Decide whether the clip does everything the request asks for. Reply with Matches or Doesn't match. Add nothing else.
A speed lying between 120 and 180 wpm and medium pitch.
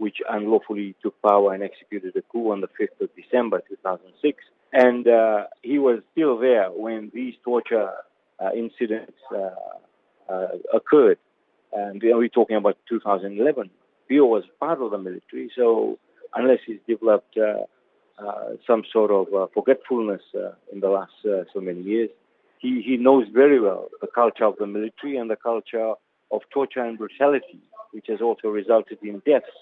Doesn't match